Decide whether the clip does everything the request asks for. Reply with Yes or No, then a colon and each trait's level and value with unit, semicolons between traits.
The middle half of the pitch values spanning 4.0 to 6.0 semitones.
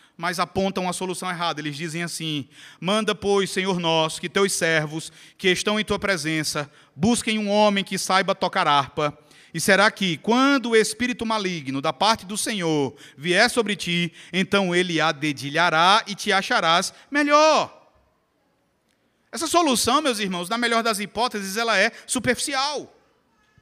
Yes: average, 5.2 semitones